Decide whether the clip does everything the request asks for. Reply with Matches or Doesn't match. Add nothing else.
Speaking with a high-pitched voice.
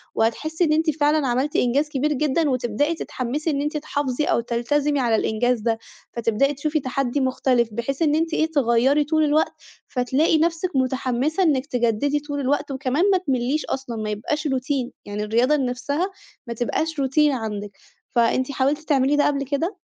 Matches